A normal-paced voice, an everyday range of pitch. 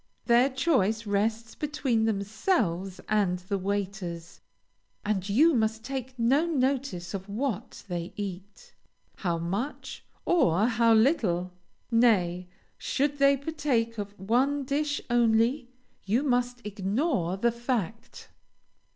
No: slow, 115 wpm; average, 5.0 semitones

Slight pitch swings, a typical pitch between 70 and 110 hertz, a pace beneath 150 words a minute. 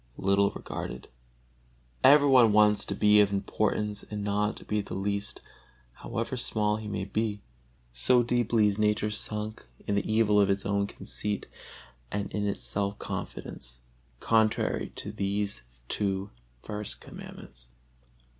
Yes: narrow, 1.2 semitones; low, 105 Hz; average, 140 wpm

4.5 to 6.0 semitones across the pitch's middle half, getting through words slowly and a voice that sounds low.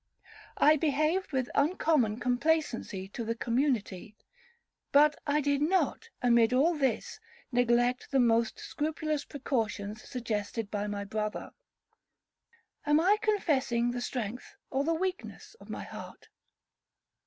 No: average, 4.8 semitones; slow, 120 wpm; very high, 255 Hz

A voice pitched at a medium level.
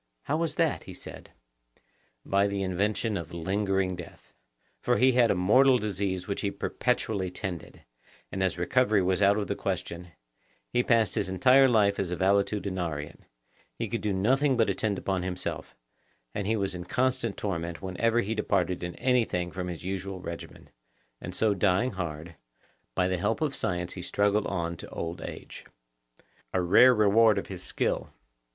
No: low, 100 Hz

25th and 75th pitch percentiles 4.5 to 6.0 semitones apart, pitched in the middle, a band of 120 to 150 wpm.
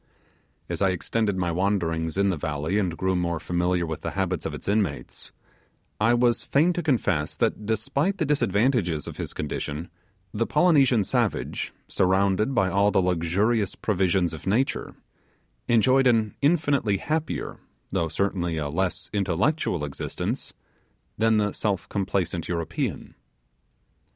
No: average, 4.8 semitones; low, 100 Hz; average, 140 wpm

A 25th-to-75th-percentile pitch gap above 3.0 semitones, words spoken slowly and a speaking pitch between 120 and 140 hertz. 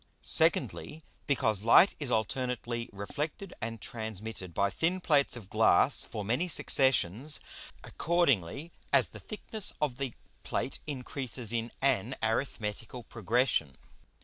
Yes: average, 4.5 semitones; slow, 120 wpm; low, 125 Hz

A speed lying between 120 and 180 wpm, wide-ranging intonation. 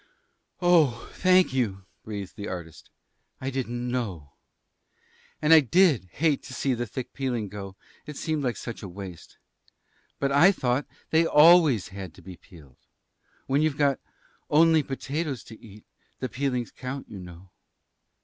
Yes: average, 150 wpm; wide, 6.7 semitones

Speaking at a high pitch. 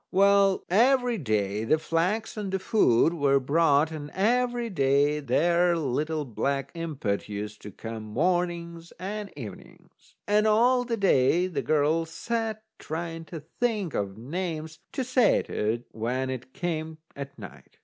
No: medium, 165 Hz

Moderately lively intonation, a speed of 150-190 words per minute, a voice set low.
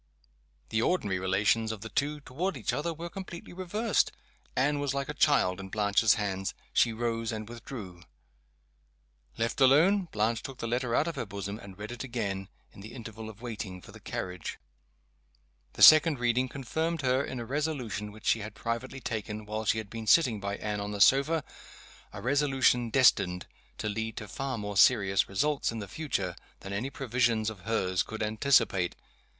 Yes: average, 4.8 semitones; average, 180 wpm; low, 115 Hz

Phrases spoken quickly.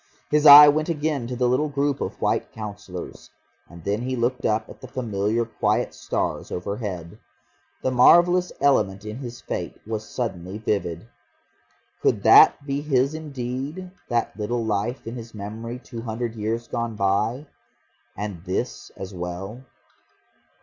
No: average, 150 wpm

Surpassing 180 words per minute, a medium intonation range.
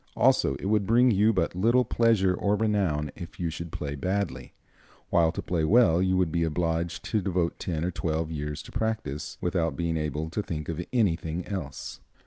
Yes: average, 190 wpm; average, 3.9 semitones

